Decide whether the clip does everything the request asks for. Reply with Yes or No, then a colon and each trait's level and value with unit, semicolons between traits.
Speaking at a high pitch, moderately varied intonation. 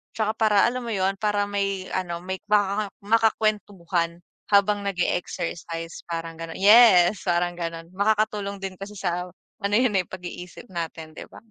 Yes: high, 195 Hz; average, 3.1 semitones